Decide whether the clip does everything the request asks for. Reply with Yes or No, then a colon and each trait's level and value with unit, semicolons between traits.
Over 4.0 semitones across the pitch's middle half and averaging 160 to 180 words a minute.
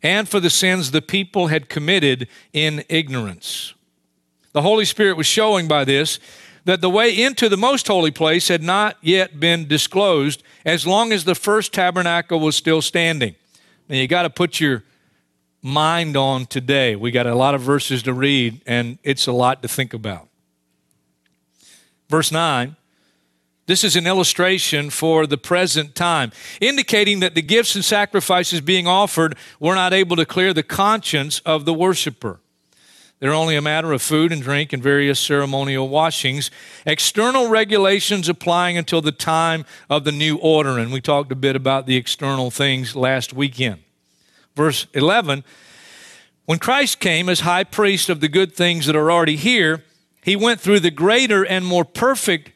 Yes: wide, 5.4 semitones; average, 170 wpm